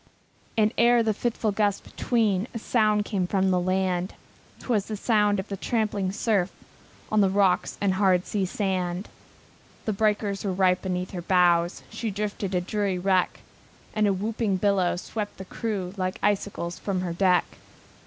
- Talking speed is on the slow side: No, average, 175 wpm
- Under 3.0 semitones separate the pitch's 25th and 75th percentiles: Yes, narrow, 2.4 semitones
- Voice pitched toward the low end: No, high, 195 Hz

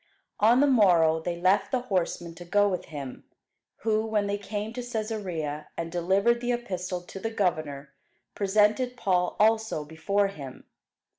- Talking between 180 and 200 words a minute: No, average, 155 wpm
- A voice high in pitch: Yes, high, 195 Hz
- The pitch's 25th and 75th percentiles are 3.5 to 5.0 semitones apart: Yes, average, 4.3 semitones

